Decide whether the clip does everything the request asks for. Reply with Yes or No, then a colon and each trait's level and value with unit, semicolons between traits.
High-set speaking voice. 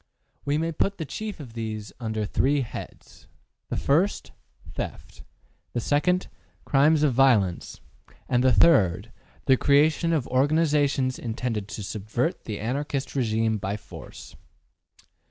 No: low, 130 Hz